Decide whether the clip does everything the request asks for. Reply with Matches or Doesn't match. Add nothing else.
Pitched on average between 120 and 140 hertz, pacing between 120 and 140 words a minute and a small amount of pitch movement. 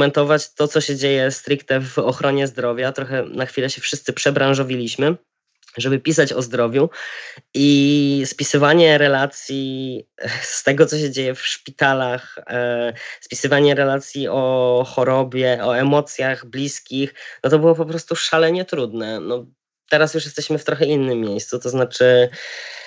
Matches